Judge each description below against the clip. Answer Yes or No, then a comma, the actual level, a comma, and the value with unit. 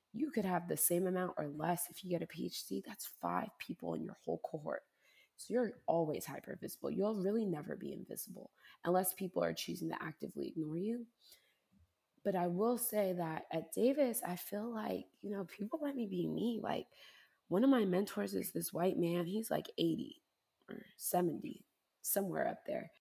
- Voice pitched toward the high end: Yes, high, 195 Hz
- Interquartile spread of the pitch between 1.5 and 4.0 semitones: No, average, 4.4 semitones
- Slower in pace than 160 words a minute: No, average, 190 wpm